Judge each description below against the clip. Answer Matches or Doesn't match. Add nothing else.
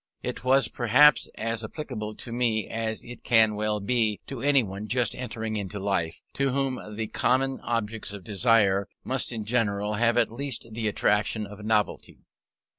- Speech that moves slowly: Doesn't match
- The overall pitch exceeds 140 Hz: Doesn't match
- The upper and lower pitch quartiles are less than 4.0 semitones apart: Matches